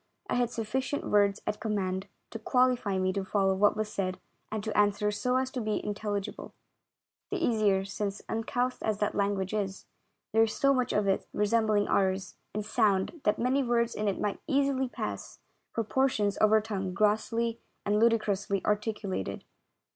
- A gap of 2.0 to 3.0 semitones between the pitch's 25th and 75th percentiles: Yes, average, 2.7 semitones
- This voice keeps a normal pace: Yes, average, 175 wpm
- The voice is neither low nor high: No, high, 210 Hz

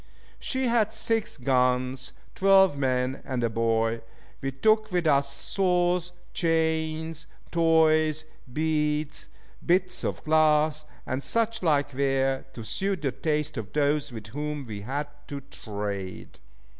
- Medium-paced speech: No, slow, 130 wpm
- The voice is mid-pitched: Yes, medium, 150 Hz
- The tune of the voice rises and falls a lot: No, average, 4.0 semitones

